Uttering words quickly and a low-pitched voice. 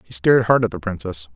Yes: fast, 265 wpm; low, 100 Hz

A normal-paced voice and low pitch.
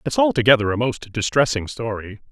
Yes: average, 155 wpm; low, 120 Hz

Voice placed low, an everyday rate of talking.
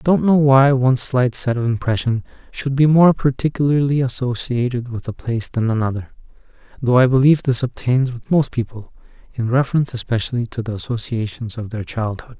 Yes: low, 125 Hz; average, 175 wpm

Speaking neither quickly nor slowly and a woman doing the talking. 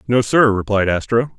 No: average, 175 wpm; male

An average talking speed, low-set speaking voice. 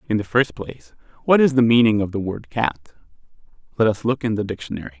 No: fast, 215 wpm; low, 110 Hz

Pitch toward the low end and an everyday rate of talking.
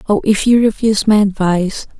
No: high, 205 Hz; average, 180 wpm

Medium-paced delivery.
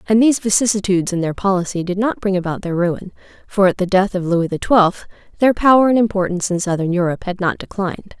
No: fast, 220 wpm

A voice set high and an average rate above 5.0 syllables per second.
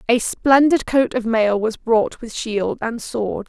No: high, 230 Hz; 3.6 syllables/s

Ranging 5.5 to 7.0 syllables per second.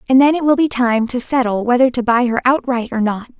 Yes: 5.8 syllables/s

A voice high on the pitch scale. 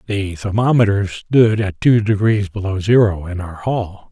No: low, 100 Hz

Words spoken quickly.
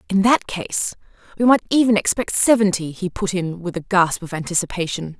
No: average, 185 wpm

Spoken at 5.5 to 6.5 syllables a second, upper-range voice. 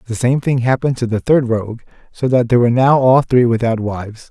No: 6.0 syllables/s; low, 120 Hz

